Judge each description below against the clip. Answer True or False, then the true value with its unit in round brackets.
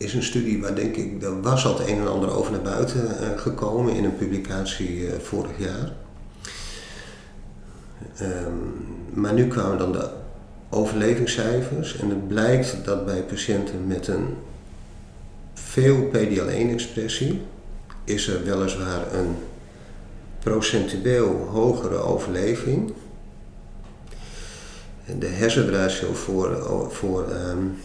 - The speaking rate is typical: False (110 wpm)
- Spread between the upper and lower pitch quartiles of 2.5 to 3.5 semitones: True (3.1 semitones)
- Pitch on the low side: True (100 Hz)